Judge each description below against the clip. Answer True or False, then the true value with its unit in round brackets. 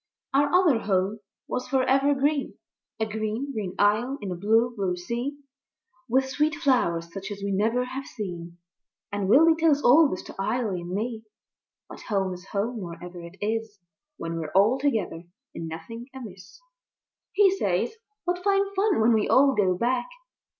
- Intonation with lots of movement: True (6.0 semitones)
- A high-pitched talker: True (225 Hz)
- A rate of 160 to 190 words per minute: True (170 wpm)